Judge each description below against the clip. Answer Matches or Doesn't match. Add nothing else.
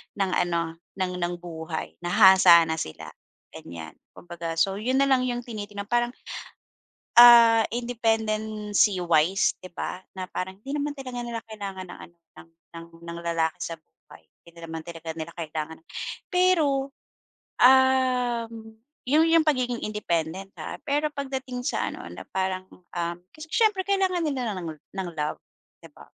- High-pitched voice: Matches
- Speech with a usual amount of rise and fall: Doesn't match